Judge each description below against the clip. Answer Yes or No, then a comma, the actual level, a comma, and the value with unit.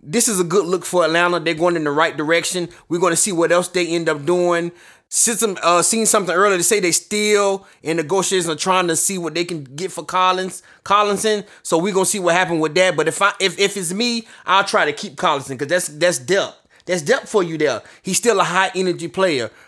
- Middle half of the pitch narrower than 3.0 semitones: Yes, narrow, 2.6 semitones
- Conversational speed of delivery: No, fast, 245 wpm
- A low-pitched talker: No, medium, 180 Hz